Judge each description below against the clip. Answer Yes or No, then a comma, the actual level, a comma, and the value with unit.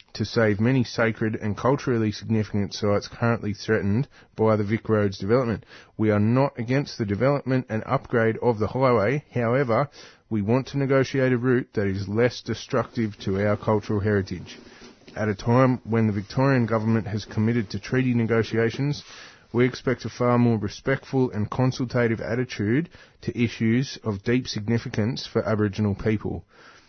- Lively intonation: No, average, 2.9 semitones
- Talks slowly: No, average, 155 wpm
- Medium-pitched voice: No, low, 115 Hz